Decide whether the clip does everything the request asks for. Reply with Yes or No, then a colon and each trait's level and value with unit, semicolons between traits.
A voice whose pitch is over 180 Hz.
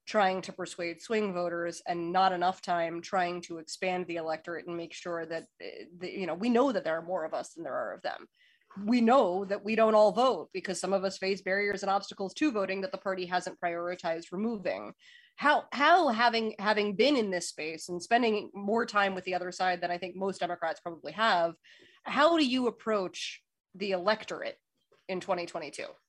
Yes: high, 190 Hz